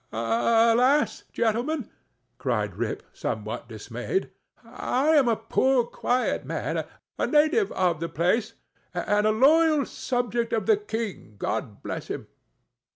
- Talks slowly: Yes, slow, 125 wpm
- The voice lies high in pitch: Yes, high, 230 Hz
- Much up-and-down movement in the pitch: Yes, wide, 8.3 semitones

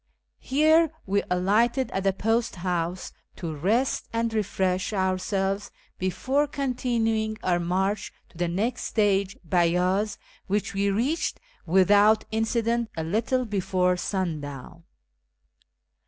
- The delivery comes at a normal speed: No, slow, 115 wpm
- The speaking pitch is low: No, high, 200 Hz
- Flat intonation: No, average, 3.7 semitones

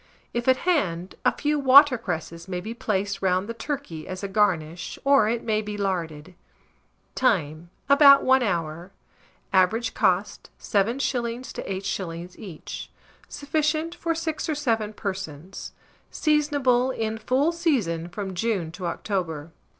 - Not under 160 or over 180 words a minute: No, slow, 135 wpm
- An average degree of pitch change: No, wide, 6.5 semitones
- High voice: Yes, high, 210 Hz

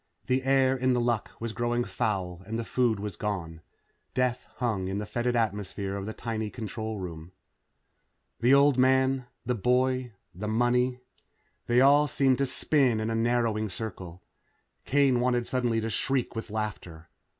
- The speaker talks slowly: No, average, 160 wpm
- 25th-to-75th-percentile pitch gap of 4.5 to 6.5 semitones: No, average, 3.3 semitones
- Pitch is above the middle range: No, low, 120 Hz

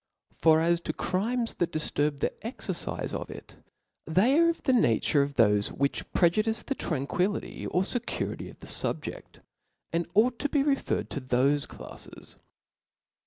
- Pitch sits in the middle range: Yes, medium, 175 Hz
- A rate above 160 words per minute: No, average, 155 wpm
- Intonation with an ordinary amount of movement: No, wide, 8.6 semitones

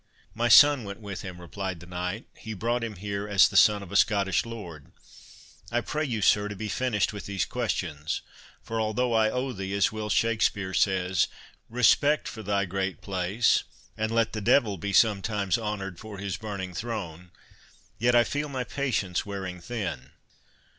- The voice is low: Yes, low, 105 Hz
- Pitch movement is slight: No, average, 3.2 semitones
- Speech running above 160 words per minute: Yes, average, 175 wpm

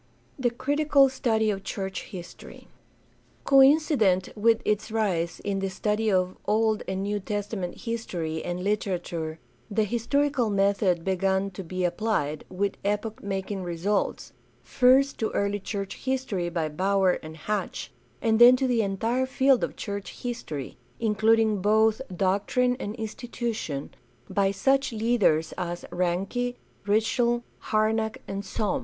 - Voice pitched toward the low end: No, high, 210 Hz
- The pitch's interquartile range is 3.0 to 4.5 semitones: Yes, average, 3.5 semitones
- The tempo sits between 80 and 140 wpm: Yes, slow, 135 wpm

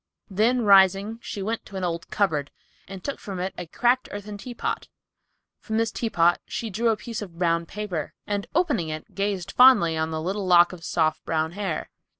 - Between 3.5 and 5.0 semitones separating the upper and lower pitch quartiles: Yes, average, 4.4 semitones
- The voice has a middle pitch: No, high, 195 Hz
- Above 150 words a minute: Yes, average, 190 wpm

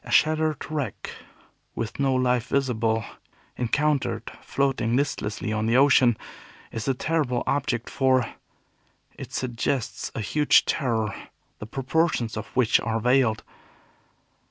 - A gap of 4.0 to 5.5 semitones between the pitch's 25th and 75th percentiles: No, average, 3.5 semitones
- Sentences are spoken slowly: Yes, slow, 120 wpm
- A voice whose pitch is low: Yes, low, 125 Hz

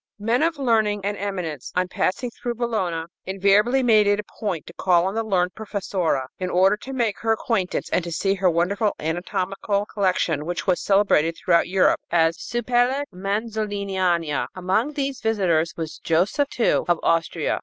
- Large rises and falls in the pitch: No, average, 3.9 semitones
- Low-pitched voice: No, high, 195 Hz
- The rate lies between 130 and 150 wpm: No, average, 165 wpm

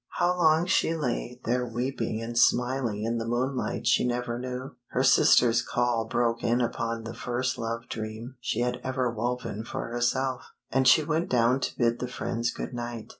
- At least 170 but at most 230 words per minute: Yes, average, 180 wpm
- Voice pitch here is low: Yes, low, 120 Hz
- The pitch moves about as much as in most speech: No, narrow, 1.7 semitones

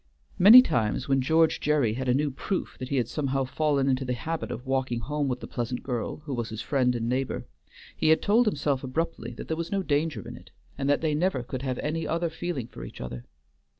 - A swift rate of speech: Yes, fast, 235 wpm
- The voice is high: No, low, 135 Hz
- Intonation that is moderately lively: Yes, average, 4.1 semitones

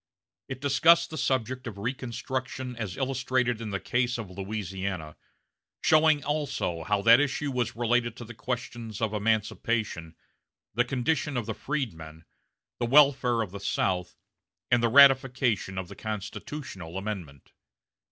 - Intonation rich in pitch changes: No, average, 4.5 semitones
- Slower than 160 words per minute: Yes, average, 140 wpm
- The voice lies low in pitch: Yes, low, 120 Hz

